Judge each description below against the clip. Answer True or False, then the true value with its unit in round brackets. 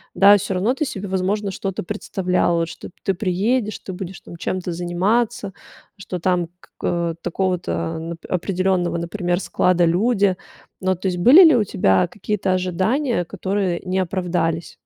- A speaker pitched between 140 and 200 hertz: True (185 Hz)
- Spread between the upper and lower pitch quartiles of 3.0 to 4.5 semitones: False (2.4 semitones)